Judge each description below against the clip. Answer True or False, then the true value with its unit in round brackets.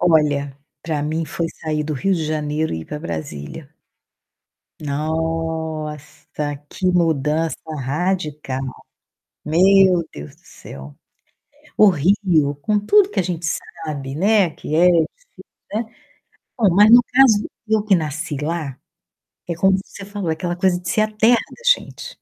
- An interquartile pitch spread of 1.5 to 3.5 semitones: False (4.3 semitones)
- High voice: False (165 Hz)